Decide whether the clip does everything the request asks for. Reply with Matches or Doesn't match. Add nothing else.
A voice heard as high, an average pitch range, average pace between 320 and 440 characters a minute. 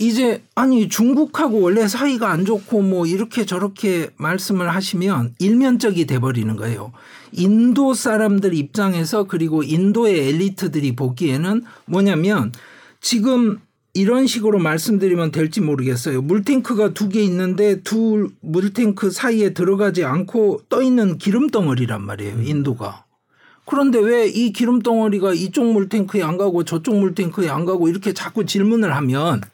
Matches